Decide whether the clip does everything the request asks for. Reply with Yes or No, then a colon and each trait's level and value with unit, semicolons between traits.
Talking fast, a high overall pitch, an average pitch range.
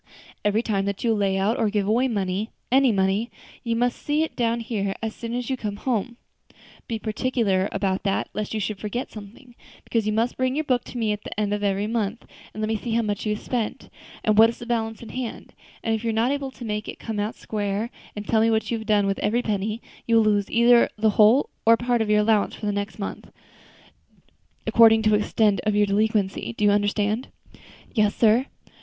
No: fast, 235 wpm; high, 220 Hz; narrow, 2.2 semitones